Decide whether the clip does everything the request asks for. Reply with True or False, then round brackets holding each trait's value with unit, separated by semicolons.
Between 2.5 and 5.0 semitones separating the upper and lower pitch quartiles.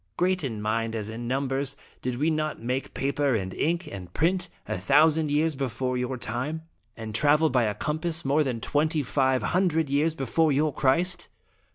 True (4.2 semitones)